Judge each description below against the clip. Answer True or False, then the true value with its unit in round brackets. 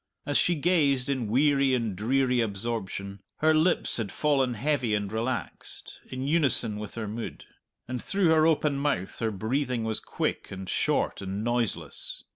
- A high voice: False (125 Hz)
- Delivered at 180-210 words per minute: False (160 wpm)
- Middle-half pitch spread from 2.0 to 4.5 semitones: False (4.9 semitones)